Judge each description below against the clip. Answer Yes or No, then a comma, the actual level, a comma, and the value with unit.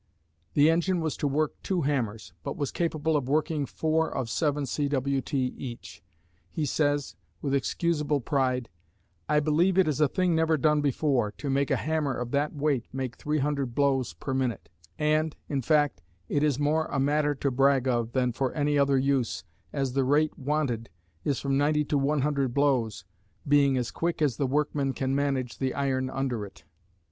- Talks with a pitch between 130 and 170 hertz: Yes, medium, 140 Hz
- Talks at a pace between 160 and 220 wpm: Yes, average, 180 wpm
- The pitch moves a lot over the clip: No, narrow, 2.4 semitones